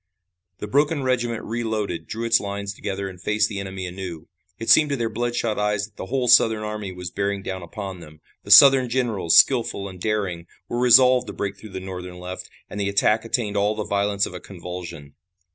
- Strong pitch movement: No, average, 3.5 semitones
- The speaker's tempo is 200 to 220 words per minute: Yes, fast, 205 wpm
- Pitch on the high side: No, low, 105 Hz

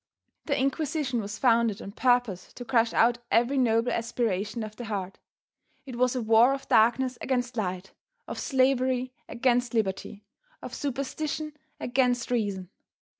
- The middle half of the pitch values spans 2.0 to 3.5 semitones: Yes, average, 2.8 semitones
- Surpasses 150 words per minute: No, average, 140 wpm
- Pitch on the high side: Yes, high, 240 Hz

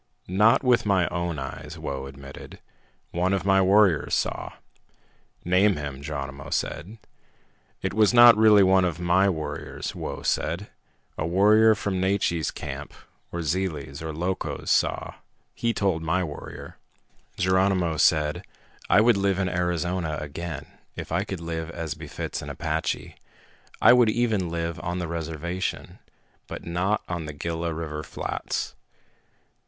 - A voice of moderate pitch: No, very low, 85 Hz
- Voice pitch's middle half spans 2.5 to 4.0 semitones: Yes, average, 3.6 semitones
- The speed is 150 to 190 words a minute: No, average, 140 wpm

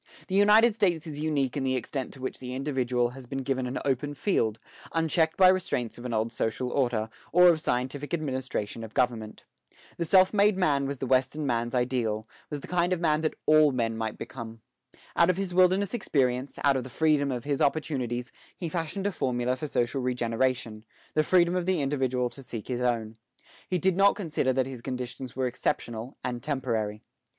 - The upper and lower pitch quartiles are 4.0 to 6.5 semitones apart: Yes, average, 4.5 semitones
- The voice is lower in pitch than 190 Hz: Yes, low, 135 Hz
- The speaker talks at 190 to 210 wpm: Yes, average, 195 wpm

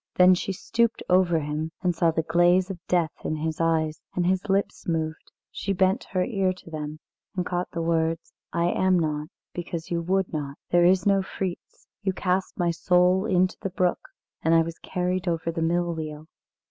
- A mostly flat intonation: Yes, narrow, 2.2 semitones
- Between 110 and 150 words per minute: No, average, 195 wpm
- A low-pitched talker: No, medium, 175 Hz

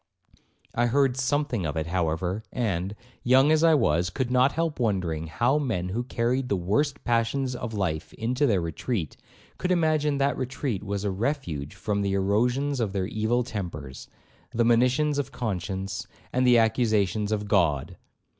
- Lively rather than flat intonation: Yes, wide, 5.7 semitones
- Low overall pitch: Yes, low, 115 Hz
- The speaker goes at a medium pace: Yes, average, 165 wpm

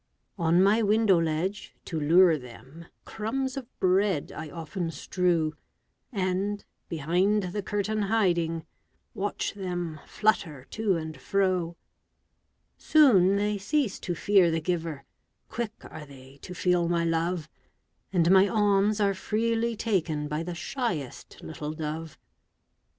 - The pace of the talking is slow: Yes, slow, 130 wpm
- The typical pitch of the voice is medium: Yes, medium, 180 Hz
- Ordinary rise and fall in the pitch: Yes, average, 4.2 semitones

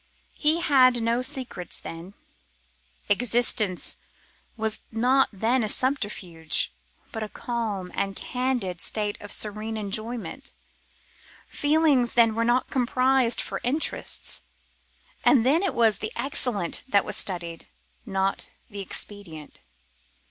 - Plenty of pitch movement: No, average, 4.1 semitones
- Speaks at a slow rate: Yes, slow, 115 wpm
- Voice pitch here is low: No, high, 225 Hz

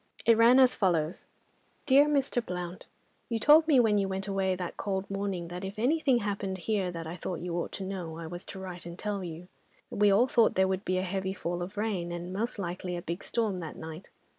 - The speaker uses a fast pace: Yes, fast, 225 wpm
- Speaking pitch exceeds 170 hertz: Yes, high, 190 Hz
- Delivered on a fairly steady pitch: No, average, 3.5 semitones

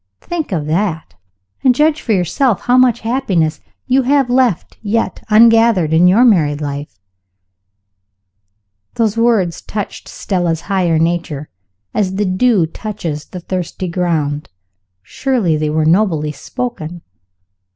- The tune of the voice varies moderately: No, wide, 6.3 semitones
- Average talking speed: No, slow, 130 wpm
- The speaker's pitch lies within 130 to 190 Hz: Yes, medium, 185 Hz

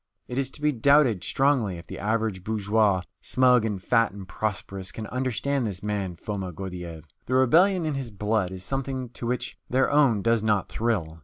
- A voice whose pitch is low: Yes, low, 110 Hz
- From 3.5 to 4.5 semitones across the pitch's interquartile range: No, average, 4.9 semitones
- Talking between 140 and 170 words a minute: No, average, 185 wpm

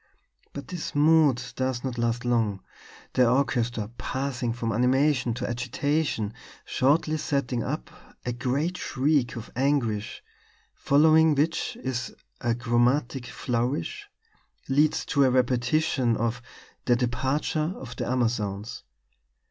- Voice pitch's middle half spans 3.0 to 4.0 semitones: Yes, average, 3.3 semitones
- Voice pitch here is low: Yes, low, 125 Hz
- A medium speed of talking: No, slow, 115 wpm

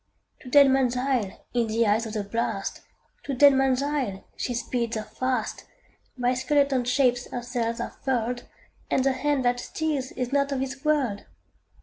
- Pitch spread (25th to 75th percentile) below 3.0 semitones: Yes, narrow, 2.4 semitones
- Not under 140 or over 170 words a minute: Yes, average, 165 wpm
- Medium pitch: No, very high, 255 Hz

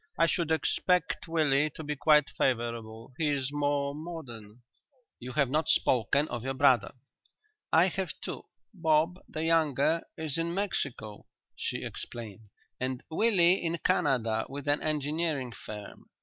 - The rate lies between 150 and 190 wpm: No, average, 140 wpm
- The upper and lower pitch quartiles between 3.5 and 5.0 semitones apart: Yes, average, 4.6 semitones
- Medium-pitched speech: Yes, medium, 145 Hz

